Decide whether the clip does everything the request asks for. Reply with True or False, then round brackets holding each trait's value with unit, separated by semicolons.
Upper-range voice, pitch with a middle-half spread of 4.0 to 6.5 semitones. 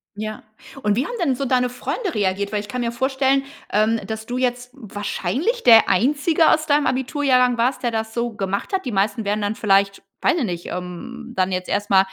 True (235 Hz; 4.3 semitones)